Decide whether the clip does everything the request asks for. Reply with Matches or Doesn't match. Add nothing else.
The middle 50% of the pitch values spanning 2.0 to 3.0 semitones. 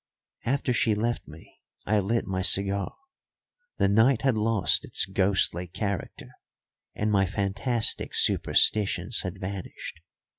Matches